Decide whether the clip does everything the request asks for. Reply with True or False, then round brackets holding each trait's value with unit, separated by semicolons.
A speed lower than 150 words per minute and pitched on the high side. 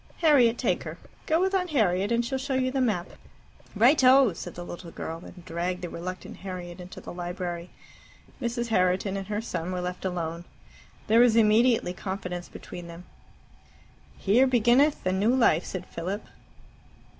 False (165 wpm; 195 Hz)